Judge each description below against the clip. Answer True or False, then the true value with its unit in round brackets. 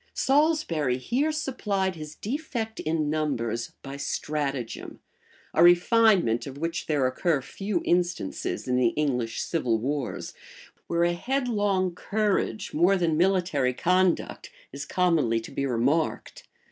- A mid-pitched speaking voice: True (165 Hz)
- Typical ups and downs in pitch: False (6.1 semitones)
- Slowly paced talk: True (125 wpm)